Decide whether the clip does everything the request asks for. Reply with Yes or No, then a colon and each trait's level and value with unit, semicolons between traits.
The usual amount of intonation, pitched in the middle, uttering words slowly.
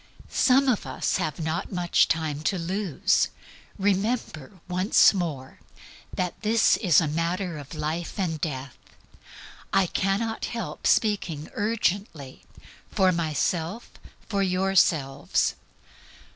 Yes: average, 4.3 semitones; medium, 180 Hz; slow, 110 wpm